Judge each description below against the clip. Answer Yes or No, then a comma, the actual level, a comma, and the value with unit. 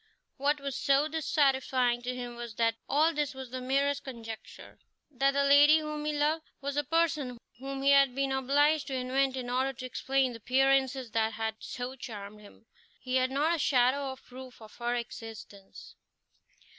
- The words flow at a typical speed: Yes, average, 180 wpm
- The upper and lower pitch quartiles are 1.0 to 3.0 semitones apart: Yes, narrow, 2.4 semitones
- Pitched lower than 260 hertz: No, very high, 265 Hz